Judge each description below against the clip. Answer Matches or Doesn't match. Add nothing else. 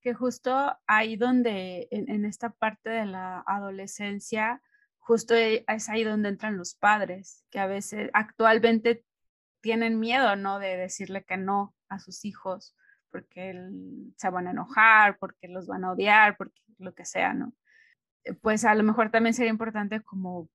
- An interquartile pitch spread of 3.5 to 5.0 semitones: Doesn't match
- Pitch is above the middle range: Matches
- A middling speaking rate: Matches